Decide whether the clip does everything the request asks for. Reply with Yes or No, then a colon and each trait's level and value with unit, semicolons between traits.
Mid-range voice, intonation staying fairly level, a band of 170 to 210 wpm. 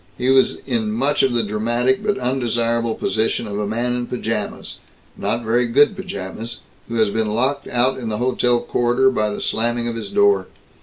No: low, 120 Hz; narrow, 2.3 semitones; average, 190 wpm